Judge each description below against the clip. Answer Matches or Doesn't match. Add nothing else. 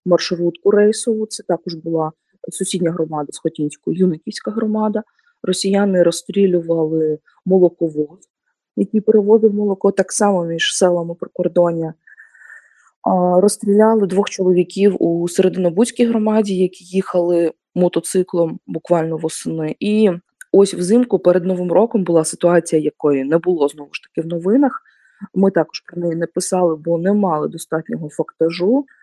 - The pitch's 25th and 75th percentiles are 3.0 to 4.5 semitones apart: Matches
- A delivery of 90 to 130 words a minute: Matches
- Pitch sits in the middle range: Matches